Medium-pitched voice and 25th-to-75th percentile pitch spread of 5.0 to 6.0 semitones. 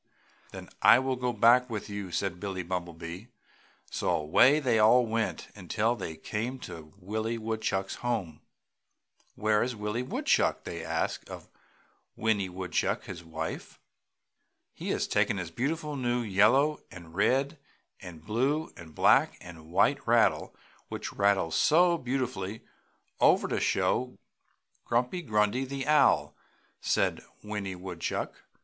No: low, 110 Hz; average, 5.3 semitones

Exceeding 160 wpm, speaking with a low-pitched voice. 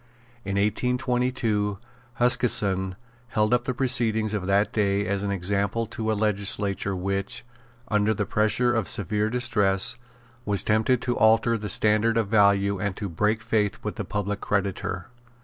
No: average, 150 wpm; low, 105 Hz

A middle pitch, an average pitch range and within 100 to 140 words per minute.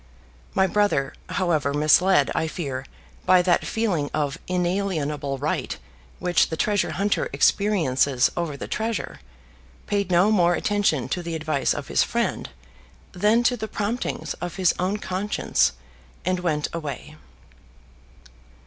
Yes: medium, 175 Hz; average, 5.0 semitones; slow, 135 wpm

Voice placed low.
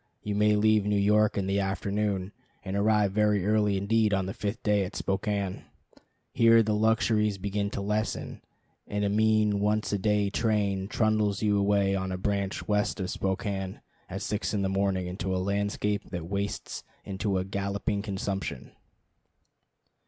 Yes: low, 100 Hz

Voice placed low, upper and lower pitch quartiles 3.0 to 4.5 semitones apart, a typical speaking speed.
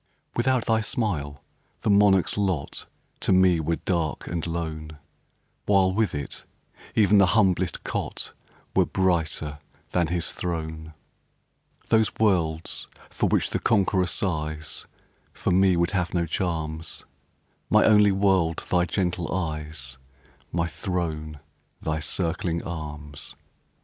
No: very low, 85 Hz; average, 3.4 semitones; slow, 120 wpm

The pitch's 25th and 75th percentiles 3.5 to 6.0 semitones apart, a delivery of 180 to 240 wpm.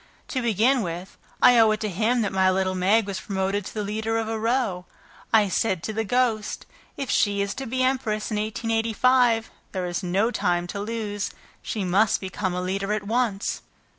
No: average, 2.9 semitones; average, 200 wpm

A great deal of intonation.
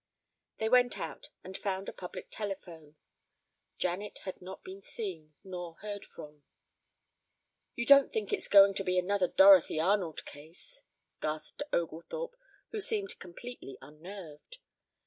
No: average, 3.9 semitones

